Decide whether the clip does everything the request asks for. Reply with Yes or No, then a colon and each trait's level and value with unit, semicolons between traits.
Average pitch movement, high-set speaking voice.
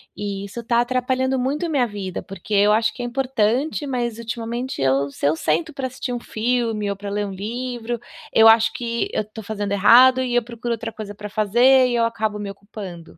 Yes: average, 3.3 semitones; high, 230 Hz